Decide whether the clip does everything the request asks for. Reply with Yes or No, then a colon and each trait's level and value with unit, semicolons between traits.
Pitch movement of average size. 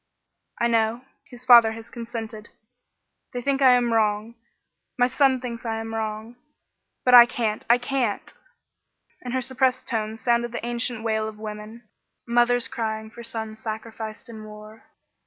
No: narrow, 1.9 semitones